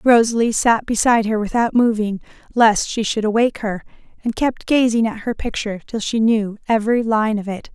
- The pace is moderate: Yes, average, 185 wpm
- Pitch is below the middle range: No, high, 225 Hz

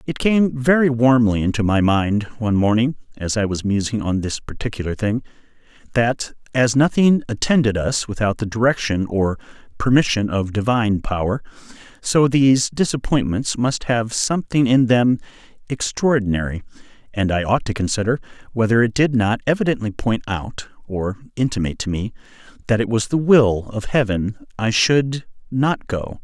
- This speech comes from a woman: No, male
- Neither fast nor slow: Yes, average, 150 wpm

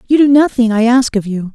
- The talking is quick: Yes, fast, 270 wpm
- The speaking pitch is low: No, high, 240 Hz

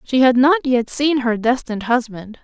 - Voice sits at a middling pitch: No, very high, 250 Hz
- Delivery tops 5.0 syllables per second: No, 4.7 syllables/s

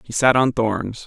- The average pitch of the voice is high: No, low, 120 Hz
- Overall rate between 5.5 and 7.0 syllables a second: No, 4.1 syllables/s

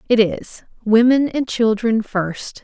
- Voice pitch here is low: No, high, 225 Hz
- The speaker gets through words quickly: No, slow, 135 wpm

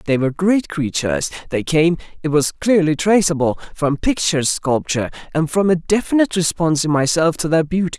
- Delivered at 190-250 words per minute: No, average, 165 wpm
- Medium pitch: Yes, medium, 160 Hz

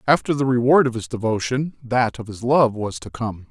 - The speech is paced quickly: Yes, fast, 225 wpm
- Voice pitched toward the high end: No, low, 125 Hz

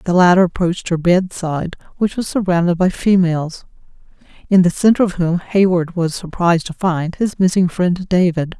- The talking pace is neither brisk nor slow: Yes, average, 165 wpm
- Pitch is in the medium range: Yes, medium, 180 Hz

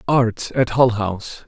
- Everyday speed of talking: Yes, average, 165 wpm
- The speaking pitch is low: Yes, low, 115 Hz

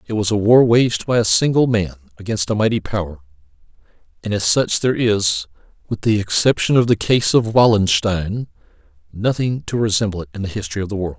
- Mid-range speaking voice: No, low, 105 Hz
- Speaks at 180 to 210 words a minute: Yes, average, 195 wpm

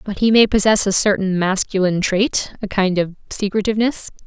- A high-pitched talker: Yes, high, 200 Hz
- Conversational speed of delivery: Yes, average, 170 wpm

